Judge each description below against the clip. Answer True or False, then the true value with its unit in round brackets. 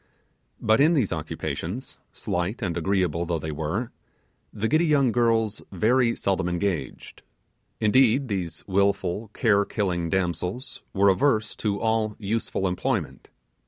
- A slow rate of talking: True (125 wpm)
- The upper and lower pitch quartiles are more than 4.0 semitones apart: True (4.4 semitones)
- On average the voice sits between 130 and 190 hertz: False (100 Hz)